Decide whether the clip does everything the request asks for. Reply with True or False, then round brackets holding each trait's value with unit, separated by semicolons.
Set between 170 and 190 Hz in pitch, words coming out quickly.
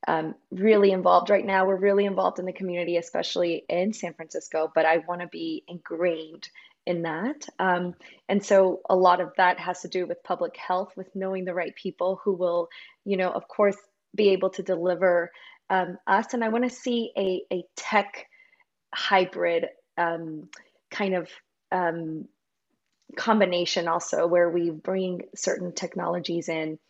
False (185 Hz; 165 wpm)